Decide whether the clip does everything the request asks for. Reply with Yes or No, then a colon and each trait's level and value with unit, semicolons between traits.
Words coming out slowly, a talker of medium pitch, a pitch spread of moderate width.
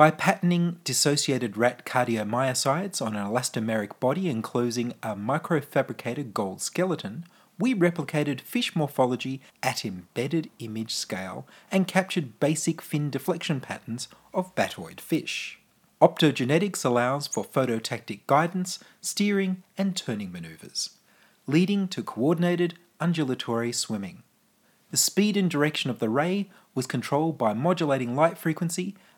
No: slow, 120 wpm; medium, 155 Hz; wide, 6.7 semitones